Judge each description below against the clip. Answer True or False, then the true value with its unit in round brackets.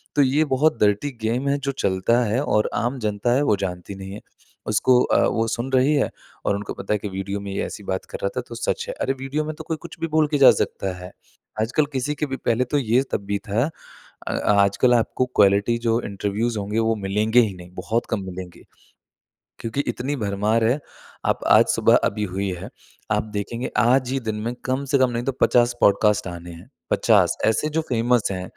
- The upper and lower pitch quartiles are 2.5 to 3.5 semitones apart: False (4.4 semitones)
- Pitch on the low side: True (115 Hz)